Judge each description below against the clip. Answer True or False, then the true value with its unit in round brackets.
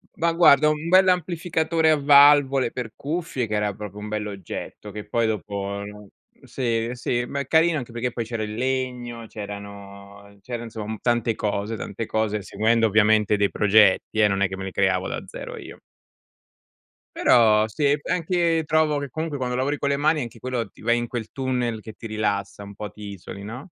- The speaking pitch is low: True (115 Hz)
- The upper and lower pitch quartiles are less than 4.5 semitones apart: False (5.1 semitones)